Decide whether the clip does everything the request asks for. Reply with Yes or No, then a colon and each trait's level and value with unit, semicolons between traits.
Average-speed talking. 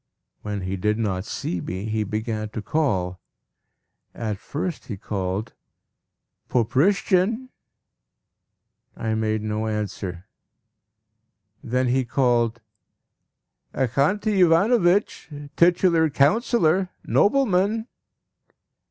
No: slow, 85 wpm